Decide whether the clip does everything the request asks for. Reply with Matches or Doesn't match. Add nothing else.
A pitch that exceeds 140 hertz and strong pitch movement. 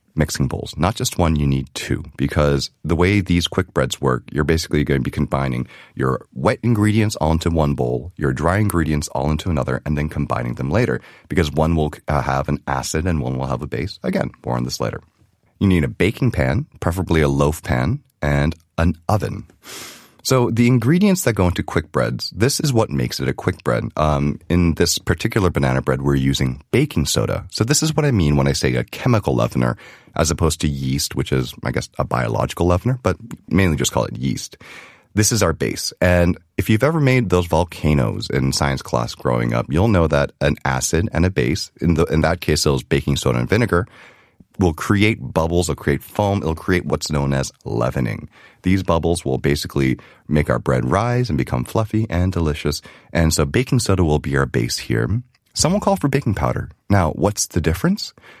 Doesn't match